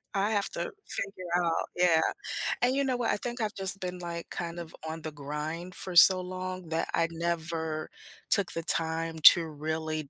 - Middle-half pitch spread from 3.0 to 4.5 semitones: No, narrow, 2.5 semitones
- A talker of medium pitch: Yes, medium, 170 Hz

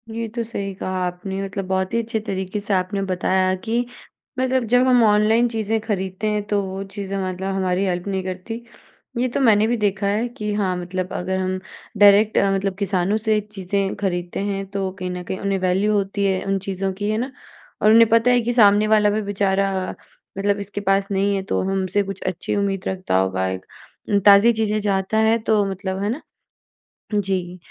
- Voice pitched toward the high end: Yes, high, 200 Hz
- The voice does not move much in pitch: Yes, narrow, 2.1 semitones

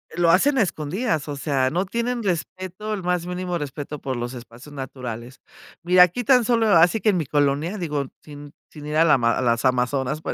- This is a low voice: No, medium, 155 Hz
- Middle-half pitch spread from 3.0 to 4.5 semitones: No, average, 5.2 semitones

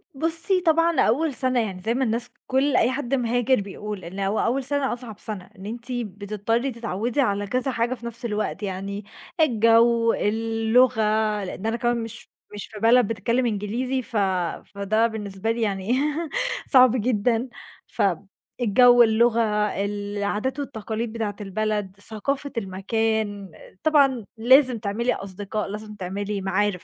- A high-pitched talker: Yes, high, 225 Hz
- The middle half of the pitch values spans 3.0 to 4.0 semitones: Yes, average, 3.5 semitones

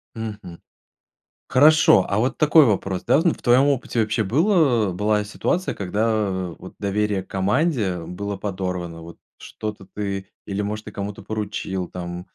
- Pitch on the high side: No, low, 105 Hz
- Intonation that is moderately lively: Yes, average, 3.2 semitones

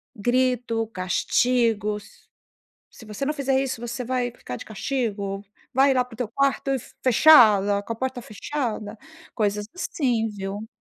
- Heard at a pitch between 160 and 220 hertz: No, high, 230 Hz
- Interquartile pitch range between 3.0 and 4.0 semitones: Yes, average, 3.7 semitones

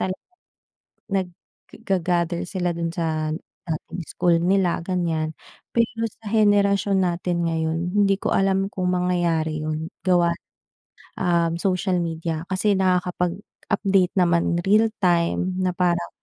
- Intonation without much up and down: Yes, narrow, 2.3 semitones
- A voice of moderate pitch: Yes, medium, 180 Hz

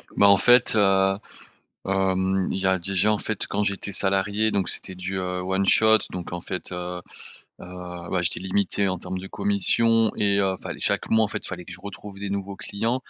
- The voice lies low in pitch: Yes, very low, 95 Hz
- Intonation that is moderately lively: No, narrow, 1.6 semitones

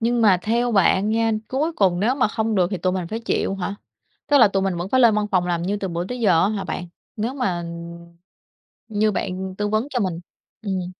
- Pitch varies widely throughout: No, average, 3.9 semitones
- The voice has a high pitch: Yes, high, 200 Hz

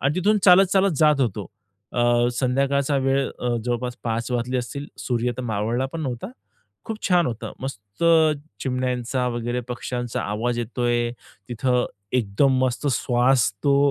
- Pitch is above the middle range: No, low, 125 Hz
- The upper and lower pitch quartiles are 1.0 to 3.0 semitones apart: Yes, narrow, 2.4 semitones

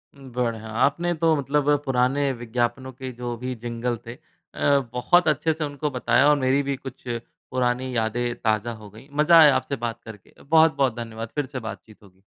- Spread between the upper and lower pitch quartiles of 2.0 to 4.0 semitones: Yes, average, 3.3 semitones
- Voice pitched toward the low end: Yes, low, 125 Hz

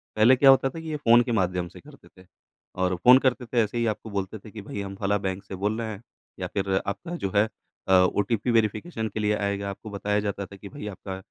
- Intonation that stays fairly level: No, average, 3.1 semitones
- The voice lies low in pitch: Yes, low, 105 Hz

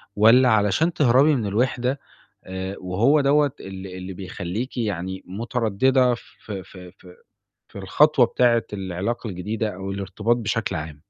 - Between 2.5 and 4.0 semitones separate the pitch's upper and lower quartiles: No, average, 4.7 semitones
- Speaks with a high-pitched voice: No, low, 105 Hz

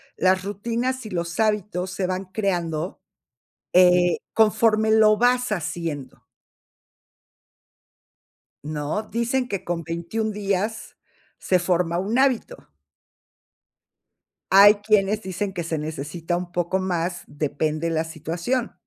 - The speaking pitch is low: No, medium, 185 Hz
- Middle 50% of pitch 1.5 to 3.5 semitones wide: No, average, 4.2 semitones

